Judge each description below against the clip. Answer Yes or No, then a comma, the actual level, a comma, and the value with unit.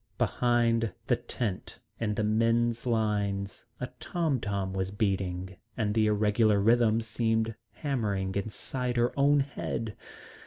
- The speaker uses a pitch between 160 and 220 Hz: No, low, 110 Hz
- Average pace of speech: No, slow, 125 wpm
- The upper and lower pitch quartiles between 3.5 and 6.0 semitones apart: No, average, 2.7 semitones